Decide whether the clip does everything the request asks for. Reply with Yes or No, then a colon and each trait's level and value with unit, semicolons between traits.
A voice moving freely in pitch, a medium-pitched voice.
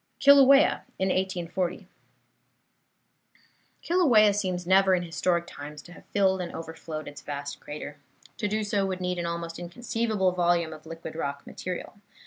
No: average, 3.4 semitones; medium, 180 Hz